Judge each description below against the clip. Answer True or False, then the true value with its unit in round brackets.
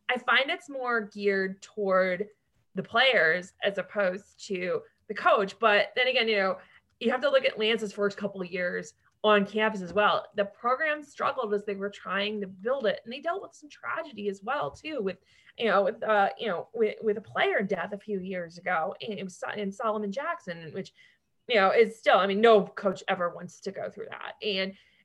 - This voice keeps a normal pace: False (210 wpm)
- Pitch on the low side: False (205 Hz)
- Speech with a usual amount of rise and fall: True (4.0 semitones)